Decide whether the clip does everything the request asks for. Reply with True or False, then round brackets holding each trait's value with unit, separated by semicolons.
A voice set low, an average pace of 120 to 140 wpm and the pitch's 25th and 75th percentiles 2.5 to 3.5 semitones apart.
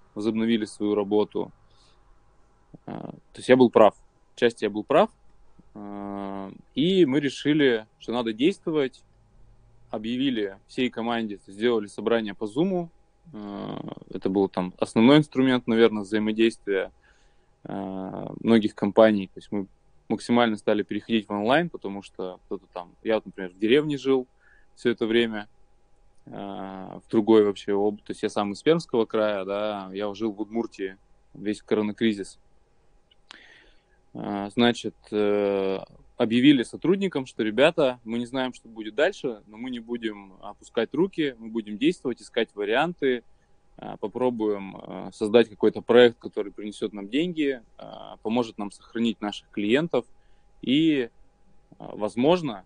True (110 Hz; 125 wpm; 2.9 semitones)